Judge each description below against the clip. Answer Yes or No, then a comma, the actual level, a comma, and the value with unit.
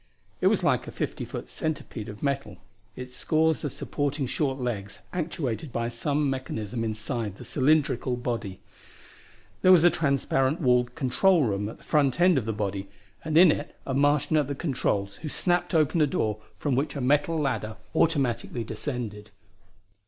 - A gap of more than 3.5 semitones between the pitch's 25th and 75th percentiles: Yes, average, 4.7 semitones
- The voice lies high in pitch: No, low, 135 Hz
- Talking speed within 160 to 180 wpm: Yes, average, 170 wpm